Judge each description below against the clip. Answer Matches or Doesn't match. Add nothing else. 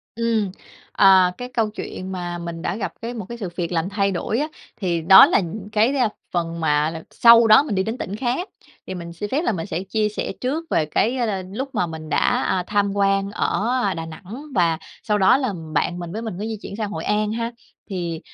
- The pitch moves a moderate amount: Matches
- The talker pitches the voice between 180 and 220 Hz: Matches